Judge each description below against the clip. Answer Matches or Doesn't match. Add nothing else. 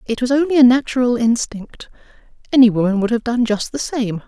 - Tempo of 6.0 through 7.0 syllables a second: Doesn't match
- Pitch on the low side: Doesn't match